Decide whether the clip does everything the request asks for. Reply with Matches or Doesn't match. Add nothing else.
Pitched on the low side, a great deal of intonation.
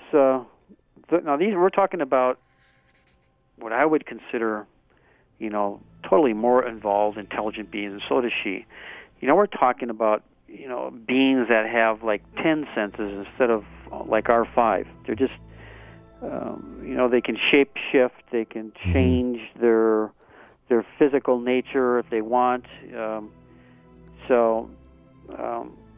Doesn't match